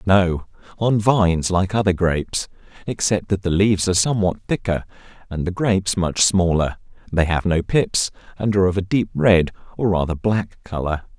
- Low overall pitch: Yes, very low, 95 Hz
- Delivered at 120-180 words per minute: Yes, average, 170 wpm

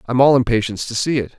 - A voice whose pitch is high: No, low, 120 Hz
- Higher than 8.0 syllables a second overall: Yes, 8.3 syllables/s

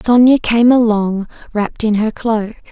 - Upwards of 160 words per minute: No, average, 155 wpm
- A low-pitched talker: No, high, 220 Hz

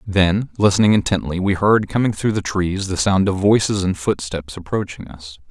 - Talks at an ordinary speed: Yes, average, 185 wpm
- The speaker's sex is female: No, male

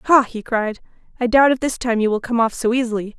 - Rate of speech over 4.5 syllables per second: Yes, 5.9 syllables/s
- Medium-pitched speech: No, high, 235 Hz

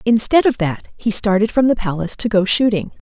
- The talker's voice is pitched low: No, high, 210 Hz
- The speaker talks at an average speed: No, fast, 215 wpm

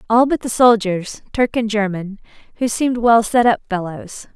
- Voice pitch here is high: Yes, high, 220 Hz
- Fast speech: No, average, 165 wpm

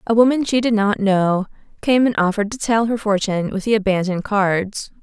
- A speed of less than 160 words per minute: No, fast, 205 wpm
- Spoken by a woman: Yes, female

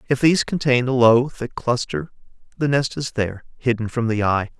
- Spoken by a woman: No, male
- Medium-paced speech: Yes, average, 195 wpm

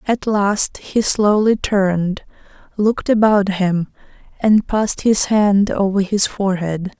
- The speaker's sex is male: No, female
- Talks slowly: Yes, slow, 130 wpm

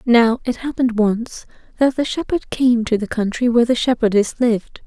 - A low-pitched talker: No, high, 235 Hz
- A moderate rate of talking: Yes, average, 185 wpm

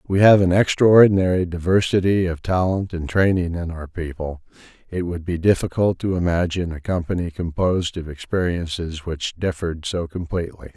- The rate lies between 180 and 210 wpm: No, average, 150 wpm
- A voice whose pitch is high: No, very low, 90 Hz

